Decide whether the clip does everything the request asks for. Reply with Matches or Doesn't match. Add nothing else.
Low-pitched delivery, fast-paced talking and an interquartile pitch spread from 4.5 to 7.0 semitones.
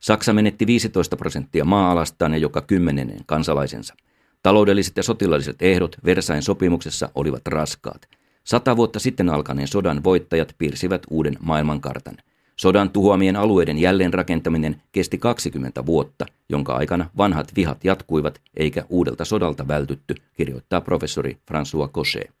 Doesn't match